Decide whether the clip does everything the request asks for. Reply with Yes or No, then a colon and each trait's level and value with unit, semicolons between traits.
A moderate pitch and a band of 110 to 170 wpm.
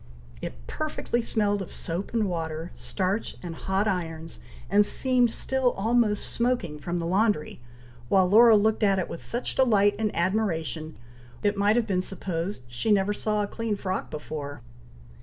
No: high, 200 Hz; average, 160 wpm